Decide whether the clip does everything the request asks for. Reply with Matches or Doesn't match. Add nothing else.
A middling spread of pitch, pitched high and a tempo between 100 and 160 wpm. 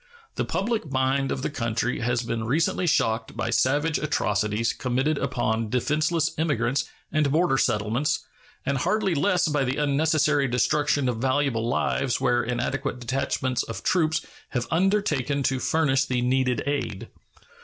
Doesn't match